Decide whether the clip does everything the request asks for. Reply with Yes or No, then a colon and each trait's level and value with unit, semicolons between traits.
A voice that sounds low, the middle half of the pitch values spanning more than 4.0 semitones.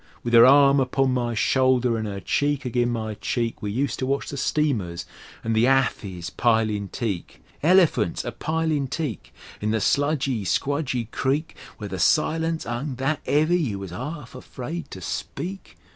Yes: low, 130 Hz; average, 4.6 semitones